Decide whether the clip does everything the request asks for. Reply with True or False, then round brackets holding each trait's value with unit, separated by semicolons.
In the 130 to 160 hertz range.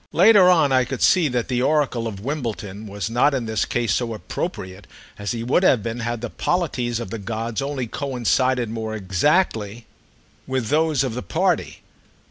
False (120 Hz)